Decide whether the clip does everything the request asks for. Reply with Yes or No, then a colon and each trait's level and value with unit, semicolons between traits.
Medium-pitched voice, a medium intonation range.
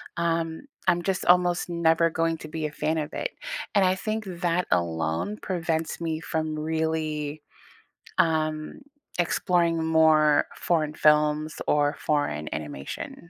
No: medium, 160 Hz; narrow, 1.9 semitones